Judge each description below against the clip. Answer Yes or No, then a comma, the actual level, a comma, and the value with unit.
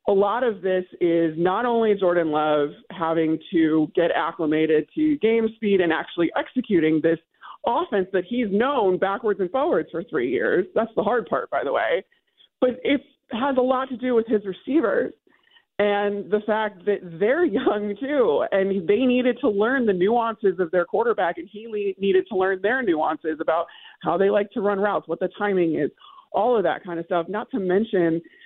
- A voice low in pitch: No, high, 205 Hz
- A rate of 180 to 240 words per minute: Yes, average, 190 wpm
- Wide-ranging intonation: Yes, wide, 5.7 semitones